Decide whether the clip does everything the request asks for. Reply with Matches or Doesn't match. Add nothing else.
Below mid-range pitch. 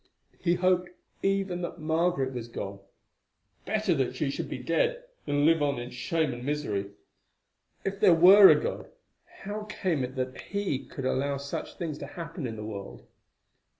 Doesn't match